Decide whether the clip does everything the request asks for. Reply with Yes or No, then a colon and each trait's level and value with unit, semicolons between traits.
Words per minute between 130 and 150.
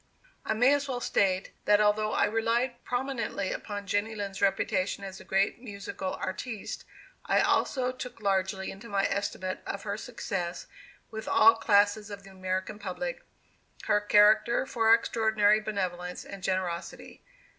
Yes: average, 145 wpm